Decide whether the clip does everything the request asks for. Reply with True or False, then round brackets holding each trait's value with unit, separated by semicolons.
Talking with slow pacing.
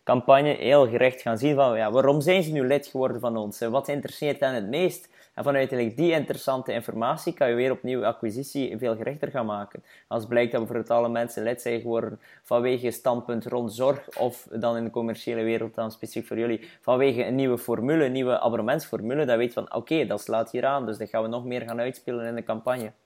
False (230 wpm)